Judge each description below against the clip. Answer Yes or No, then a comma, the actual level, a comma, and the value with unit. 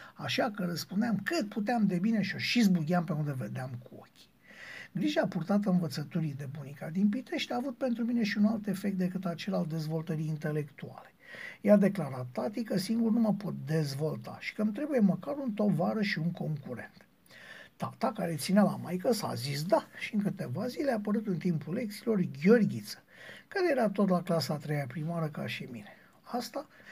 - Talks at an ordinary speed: No, fast, 190 wpm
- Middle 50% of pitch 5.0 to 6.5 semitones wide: Yes, average, 5.3 semitones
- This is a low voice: No, high, 195 Hz